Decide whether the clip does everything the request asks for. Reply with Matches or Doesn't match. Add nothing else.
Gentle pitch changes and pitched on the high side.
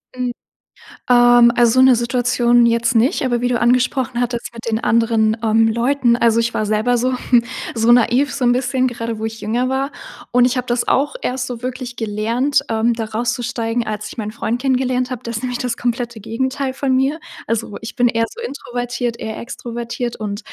Matches